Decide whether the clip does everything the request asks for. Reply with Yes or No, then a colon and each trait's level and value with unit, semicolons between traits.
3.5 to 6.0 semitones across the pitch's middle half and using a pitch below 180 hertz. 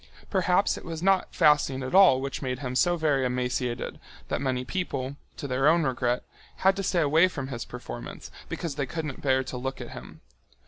Yes: average, 4.6 semitones; low, 135 Hz